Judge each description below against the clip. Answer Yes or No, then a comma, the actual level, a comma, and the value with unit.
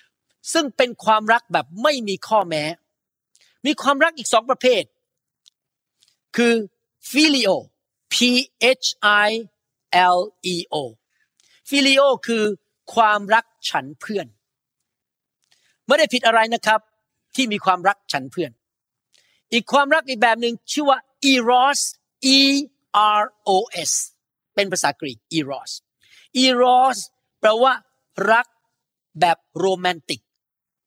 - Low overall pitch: No, high, 225 Hz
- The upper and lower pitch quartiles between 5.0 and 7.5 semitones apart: Yes, average, 5.3 semitones